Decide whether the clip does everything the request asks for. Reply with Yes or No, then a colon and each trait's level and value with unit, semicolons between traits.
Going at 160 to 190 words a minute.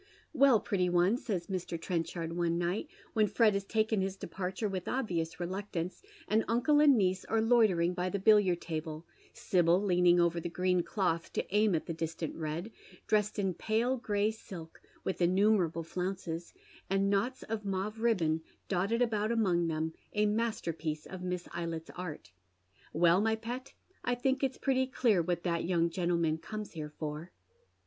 Yes: average, 170 wpm